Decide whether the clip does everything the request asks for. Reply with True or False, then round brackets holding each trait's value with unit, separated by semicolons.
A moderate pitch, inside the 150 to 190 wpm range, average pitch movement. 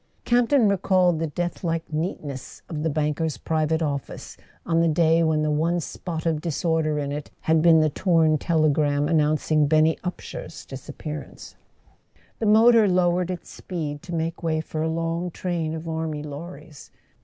False (160 Hz; 160 wpm; 2.1 semitones)